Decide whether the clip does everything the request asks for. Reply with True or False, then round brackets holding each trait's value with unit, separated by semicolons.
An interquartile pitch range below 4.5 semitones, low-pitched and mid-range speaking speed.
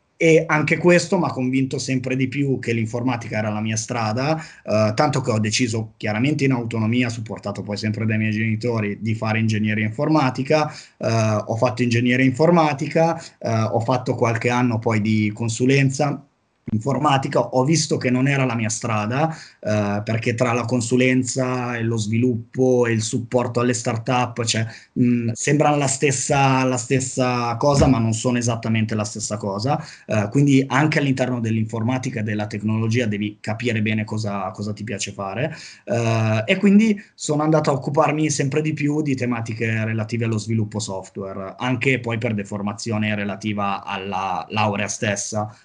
True (3.6 semitones; 120 Hz; 160 wpm)